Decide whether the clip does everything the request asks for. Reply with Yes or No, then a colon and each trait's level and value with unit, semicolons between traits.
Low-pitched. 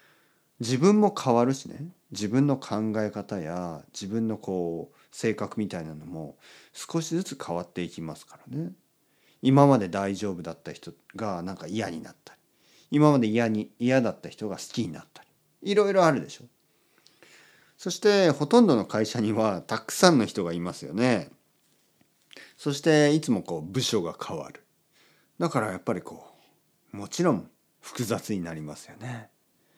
Yes: low, 115 Hz